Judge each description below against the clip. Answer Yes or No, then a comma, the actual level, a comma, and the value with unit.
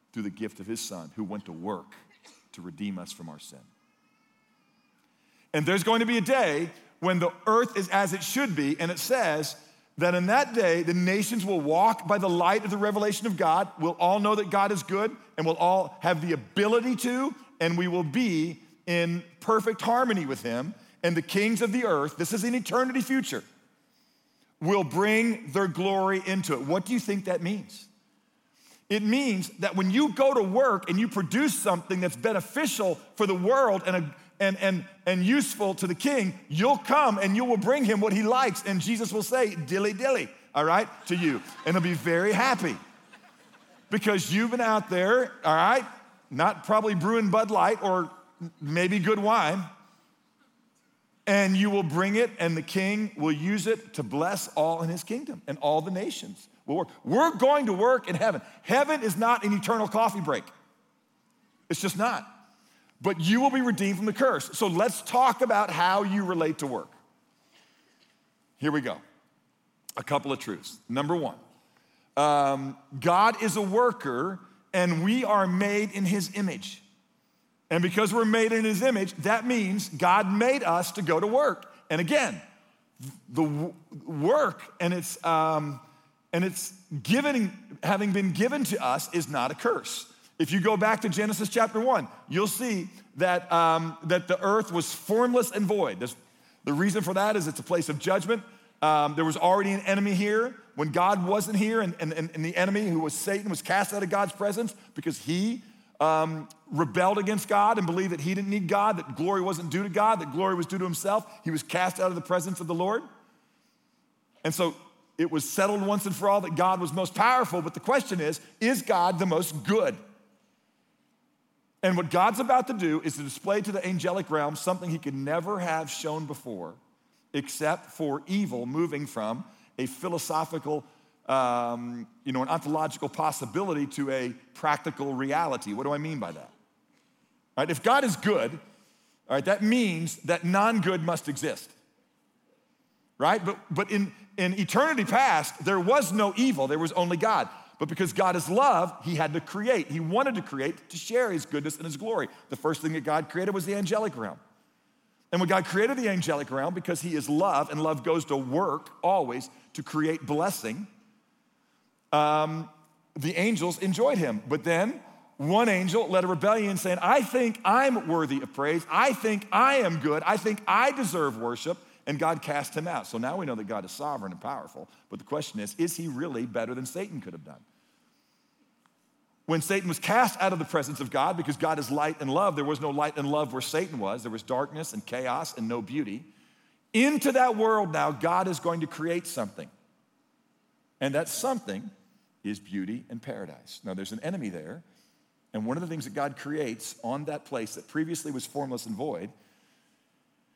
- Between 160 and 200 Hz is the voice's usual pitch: Yes, high, 190 Hz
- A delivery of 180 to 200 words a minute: Yes, average, 190 wpm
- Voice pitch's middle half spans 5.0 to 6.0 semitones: Yes, wide, 5.6 semitones